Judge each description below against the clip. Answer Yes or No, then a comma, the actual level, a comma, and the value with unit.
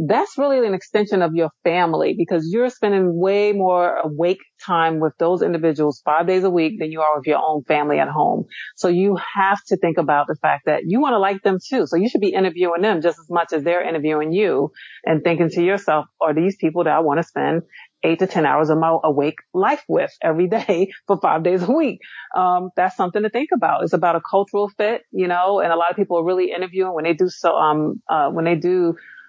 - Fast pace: Yes, fast, 240 wpm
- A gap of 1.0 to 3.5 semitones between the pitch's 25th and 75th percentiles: Yes, average, 3.1 semitones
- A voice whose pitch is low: No, medium, 175 Hz